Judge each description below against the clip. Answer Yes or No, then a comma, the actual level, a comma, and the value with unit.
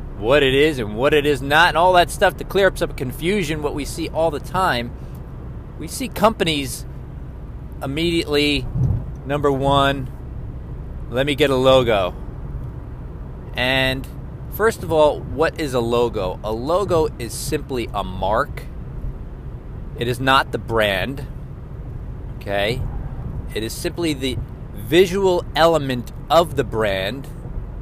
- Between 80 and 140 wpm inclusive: Yes, slow, 135 wpm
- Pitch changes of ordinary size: Yes, average, 4.4 semitones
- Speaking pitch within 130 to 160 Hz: Yes, low, 135 Hz